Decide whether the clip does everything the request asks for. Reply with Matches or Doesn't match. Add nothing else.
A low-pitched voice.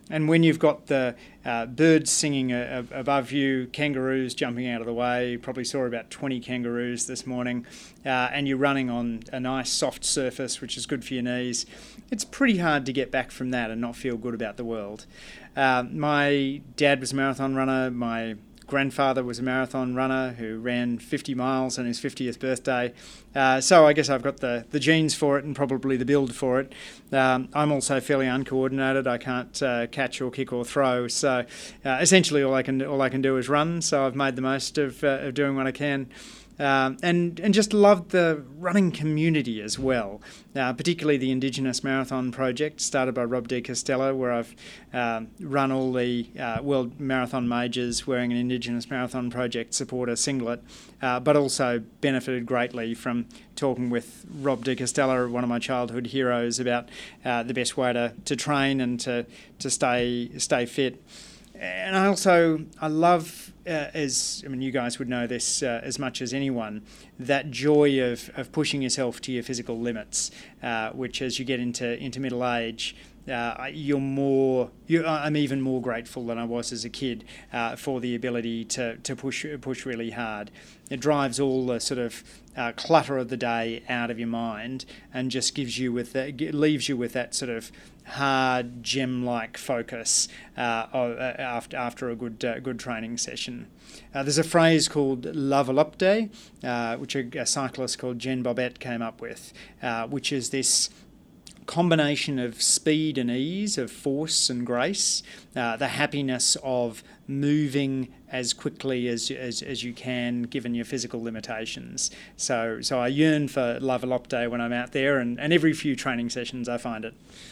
Matches